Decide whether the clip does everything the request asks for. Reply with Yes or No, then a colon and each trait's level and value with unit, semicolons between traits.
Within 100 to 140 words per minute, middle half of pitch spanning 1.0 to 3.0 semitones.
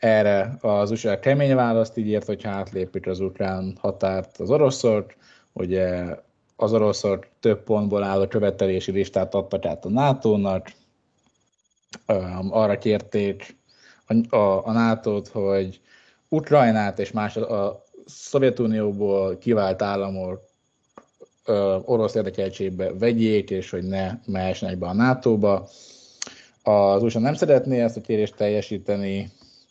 Yes: average, 120 wpm; narrow, 2.6 semitones